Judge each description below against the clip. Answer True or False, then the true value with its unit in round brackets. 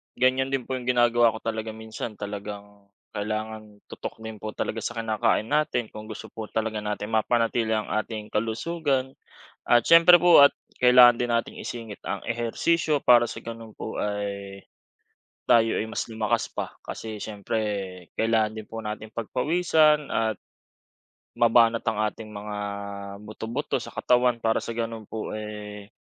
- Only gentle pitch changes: True (2.1 semitones)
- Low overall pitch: True (110 Hz)